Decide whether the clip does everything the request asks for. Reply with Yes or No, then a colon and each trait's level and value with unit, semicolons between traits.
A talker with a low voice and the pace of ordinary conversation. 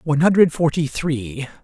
No: medium, 150 Hz; average, 145 wpm